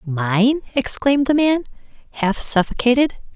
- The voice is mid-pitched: No, high, 245 Hz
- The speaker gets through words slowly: Yes, slow, 105 wpm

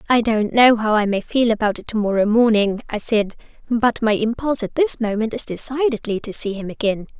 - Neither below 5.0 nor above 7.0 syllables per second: Yes, 5.5 syllables/s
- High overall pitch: Yes, high, 220 Hz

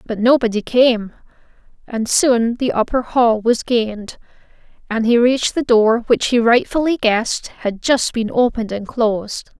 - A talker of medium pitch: No, high, 235 Hz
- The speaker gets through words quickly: No, average, 155 wpm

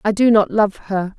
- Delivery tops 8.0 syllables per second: No, 4.6 syllables/s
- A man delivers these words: No, female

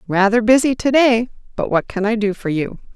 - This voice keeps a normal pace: No, fast, 225 wpm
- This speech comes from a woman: Yes, female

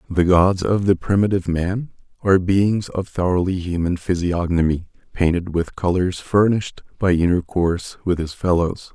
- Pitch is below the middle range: Yes, very low, 90 Hz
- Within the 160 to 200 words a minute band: No, average, 140 wpm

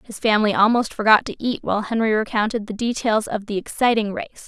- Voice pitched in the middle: No, high, 220 Hz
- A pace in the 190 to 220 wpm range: Yes, average, 200 wpm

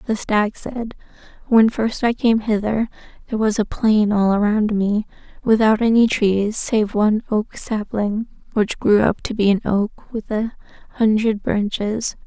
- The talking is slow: No, average, 160 wpm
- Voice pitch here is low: No, high, 215 Hz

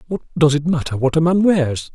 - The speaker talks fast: Yes, fast, 245 wpm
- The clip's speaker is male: Yes, male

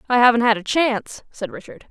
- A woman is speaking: Yes, female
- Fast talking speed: Yes, fast, 220 wpm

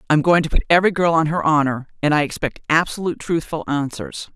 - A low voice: No, medium, 160 Hz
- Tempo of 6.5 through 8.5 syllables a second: Yes, 6.8 syllables/s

